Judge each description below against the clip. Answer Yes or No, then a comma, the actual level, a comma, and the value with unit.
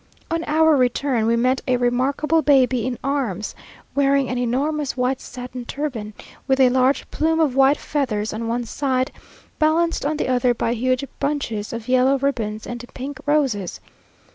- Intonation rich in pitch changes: No, average, 2.7 semitones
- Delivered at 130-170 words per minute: Yes, average, 165 wpm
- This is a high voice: Yes, very high, 255 Hz